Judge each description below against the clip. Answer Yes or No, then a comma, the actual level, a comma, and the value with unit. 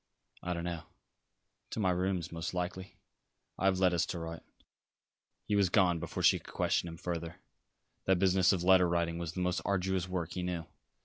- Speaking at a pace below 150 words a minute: No, average, 185 wpm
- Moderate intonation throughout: No, narrow, 1.7 semitones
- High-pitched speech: No, very low, 90 Hz